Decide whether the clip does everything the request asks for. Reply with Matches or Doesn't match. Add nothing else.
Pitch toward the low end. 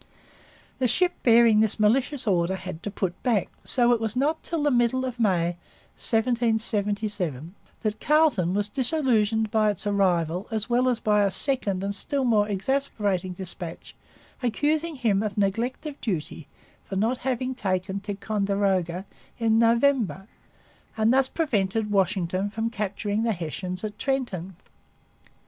Doesn't match